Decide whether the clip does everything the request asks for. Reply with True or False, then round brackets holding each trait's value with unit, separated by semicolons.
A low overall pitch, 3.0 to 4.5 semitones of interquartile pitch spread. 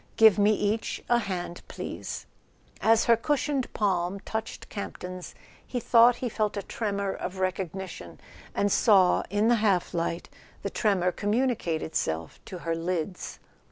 False (200 Hz; 3.6 semitones)